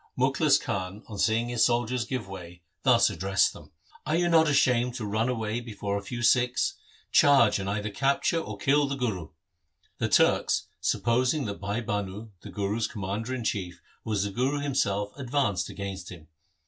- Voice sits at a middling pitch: No, low, 110 Hz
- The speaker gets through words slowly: No, average, 180 wpm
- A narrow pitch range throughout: No, average, 4.1 semitones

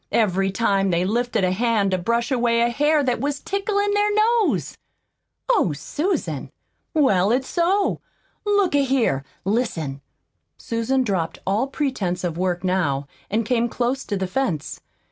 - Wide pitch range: Yes, wide, 7.0 semitones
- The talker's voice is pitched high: Yes, high, 235 Hz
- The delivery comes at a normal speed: Yes, average, 150 wpm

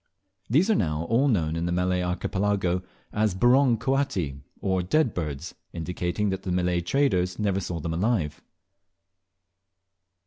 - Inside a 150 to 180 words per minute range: No, average, 140 wpm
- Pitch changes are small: No, average, 4.0 semitones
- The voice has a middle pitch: No, very low, 90 Hz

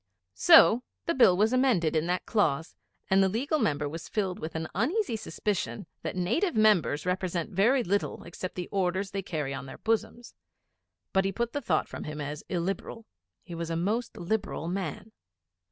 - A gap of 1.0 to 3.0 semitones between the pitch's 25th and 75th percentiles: No, average, 4.9 semitones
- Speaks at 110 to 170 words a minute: No, average, 180 wpm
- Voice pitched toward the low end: No, high, 190 Hz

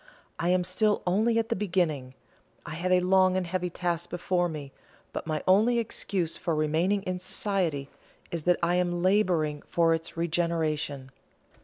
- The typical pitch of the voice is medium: Yes, medium, 175 Hz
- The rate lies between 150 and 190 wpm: Yes, average, 165 wpm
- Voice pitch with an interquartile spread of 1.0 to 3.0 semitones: Yes, narrow, 2.5 semitones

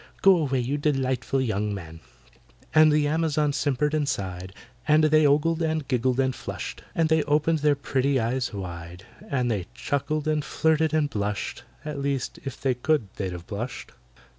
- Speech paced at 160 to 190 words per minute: Yes, average, 170 wpm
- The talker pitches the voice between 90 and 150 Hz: Yes, medium, 140 Hz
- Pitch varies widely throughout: No, average, 4.5 semitones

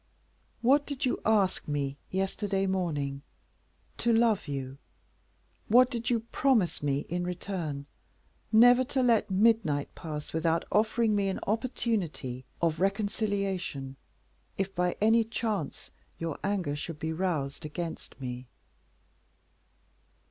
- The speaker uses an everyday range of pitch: No, wide, 6.7 semitones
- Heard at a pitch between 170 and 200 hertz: Yes, high, 190 Hz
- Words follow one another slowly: Yes, slow, 120 wpm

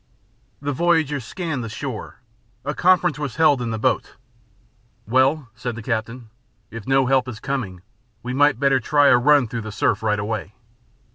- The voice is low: Yes, low, 130 Hz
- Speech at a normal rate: Yes, average, 170 wpm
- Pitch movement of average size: Yes, average, 4.2 semitones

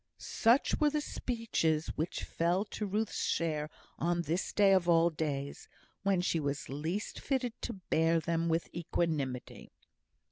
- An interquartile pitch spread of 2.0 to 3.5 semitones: No, average, 4.1 semitones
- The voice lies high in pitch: No, medium, 170 Hz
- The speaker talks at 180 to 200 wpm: No, average, 145 wpm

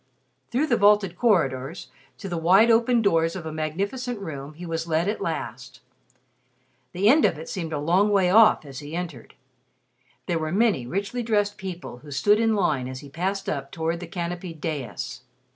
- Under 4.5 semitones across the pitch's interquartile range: No, average, 4.8 semitones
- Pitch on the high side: No, medium, 175 Hz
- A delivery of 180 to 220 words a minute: Yes, average, 185 wpm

